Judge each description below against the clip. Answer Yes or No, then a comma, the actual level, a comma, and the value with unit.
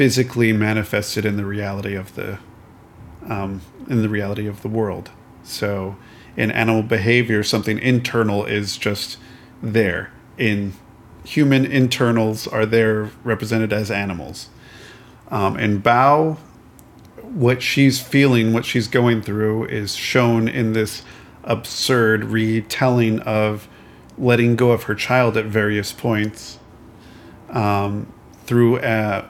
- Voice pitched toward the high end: No, low, 110 Hz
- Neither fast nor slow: No, slow, 120 wpm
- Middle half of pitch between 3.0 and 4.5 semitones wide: No, narrow, 2.5 semitones